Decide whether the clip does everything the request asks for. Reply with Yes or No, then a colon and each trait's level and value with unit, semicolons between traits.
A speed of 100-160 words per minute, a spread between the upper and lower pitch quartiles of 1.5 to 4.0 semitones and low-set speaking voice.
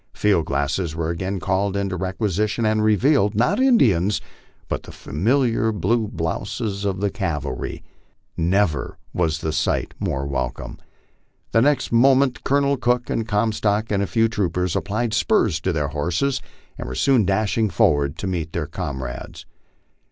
No: average, 150 wpm; average, 5.3 semitones; low, 100 Hz